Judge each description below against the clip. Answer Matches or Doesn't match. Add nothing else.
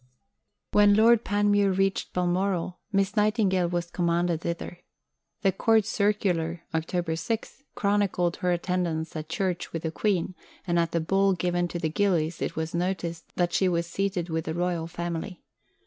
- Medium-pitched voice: Matches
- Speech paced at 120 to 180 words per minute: Matches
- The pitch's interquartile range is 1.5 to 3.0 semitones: Matches